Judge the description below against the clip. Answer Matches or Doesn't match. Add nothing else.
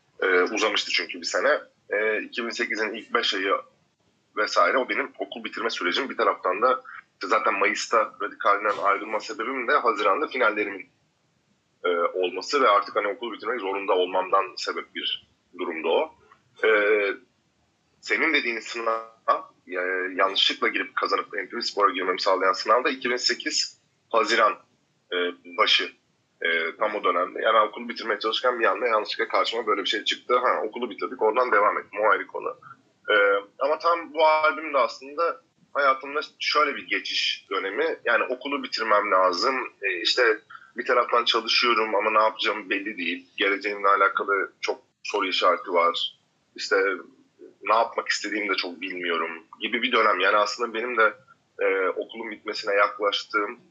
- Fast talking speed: Matches